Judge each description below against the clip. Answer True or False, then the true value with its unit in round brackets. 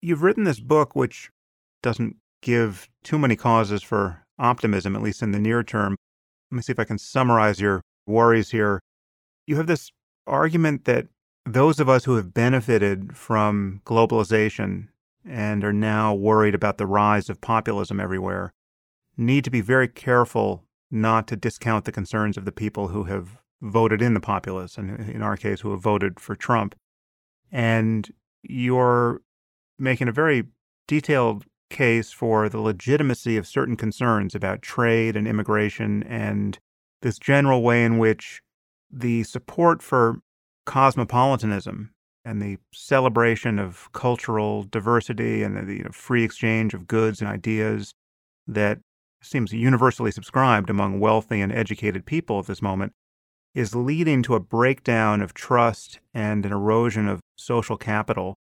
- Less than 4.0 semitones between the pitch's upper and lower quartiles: True (2.9 semitones)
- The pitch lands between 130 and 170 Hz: False (110 Hz)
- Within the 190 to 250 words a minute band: False (150 wpm)